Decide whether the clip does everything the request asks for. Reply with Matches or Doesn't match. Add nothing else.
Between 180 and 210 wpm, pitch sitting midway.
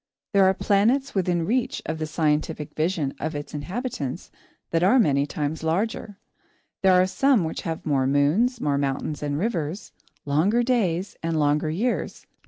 Doesn't match